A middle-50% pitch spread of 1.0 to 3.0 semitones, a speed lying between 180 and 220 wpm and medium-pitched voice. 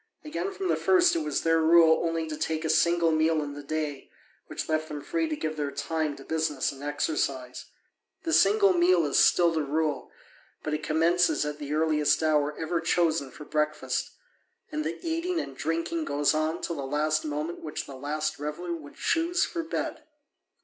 Yes: narrow, 2.5 semitones; average, 190 wpm; medium, 155 Hz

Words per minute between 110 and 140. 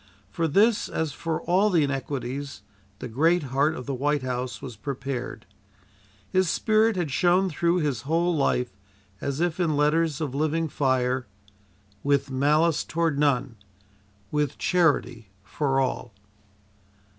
Yes: slow, 135 wpm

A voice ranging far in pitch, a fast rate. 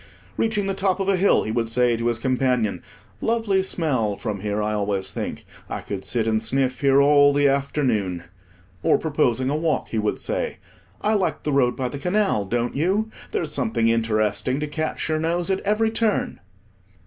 No: wide, 7.9 semitones; average, 185 wpm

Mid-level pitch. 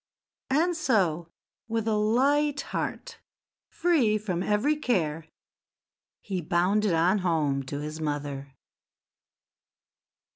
No: high, 195 Hz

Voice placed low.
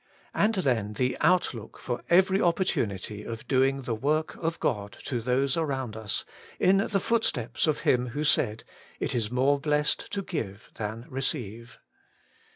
Yes: low, 130 Hz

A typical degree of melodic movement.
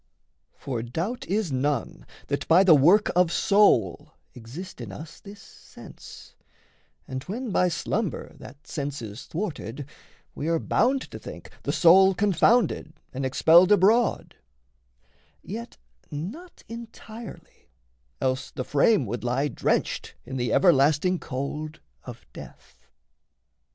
No: wide, 7.2 semitones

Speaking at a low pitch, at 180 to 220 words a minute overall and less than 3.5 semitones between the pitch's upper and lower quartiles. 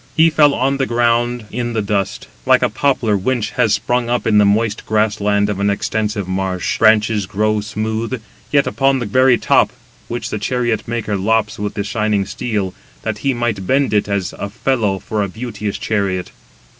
Yes: low, 110 Hz; average, 185 wpm; average, 2.9 semitones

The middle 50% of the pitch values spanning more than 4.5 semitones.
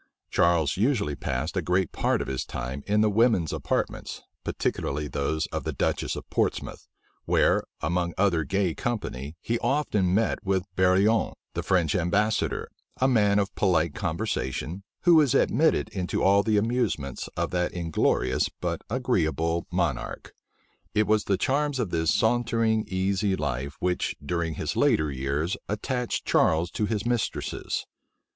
Yes: average, 5.3 semitones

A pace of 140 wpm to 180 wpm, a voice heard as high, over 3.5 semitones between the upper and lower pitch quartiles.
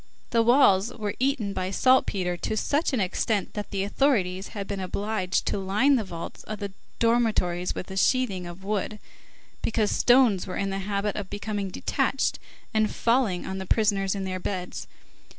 No: average, 175 wpm; high, 200 Hz; average, 3.1 semitones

